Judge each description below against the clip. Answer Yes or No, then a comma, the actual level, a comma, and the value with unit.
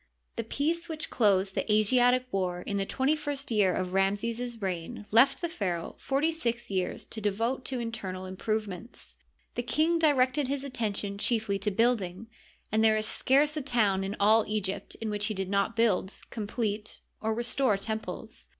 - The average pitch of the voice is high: Yes, high, 220 Hz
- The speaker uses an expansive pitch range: No, average, 4.2 semitones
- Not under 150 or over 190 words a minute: Yes, average, 175 wpm